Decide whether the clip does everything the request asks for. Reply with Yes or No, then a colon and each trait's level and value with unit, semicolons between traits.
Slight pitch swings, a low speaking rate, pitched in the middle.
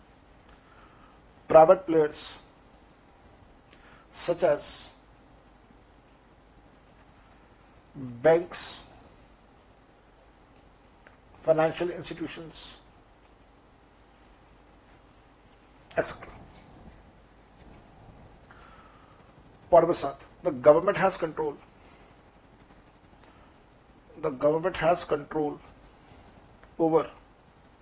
Yes: narrow, 1.9 semitones; slow, 40 wpm; medium, 160 Hz